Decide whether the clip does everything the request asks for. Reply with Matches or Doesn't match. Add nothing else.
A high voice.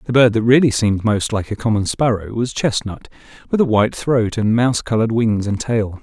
Doesn't match